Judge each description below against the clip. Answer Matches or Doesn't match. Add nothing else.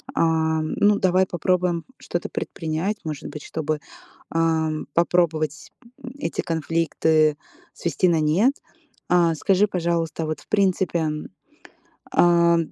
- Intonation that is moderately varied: Doesn't match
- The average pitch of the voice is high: Doesn't match